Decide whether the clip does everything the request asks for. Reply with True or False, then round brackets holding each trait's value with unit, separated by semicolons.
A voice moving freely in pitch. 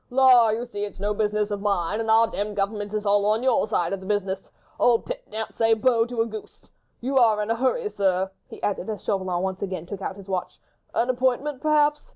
False (3.3 semitones)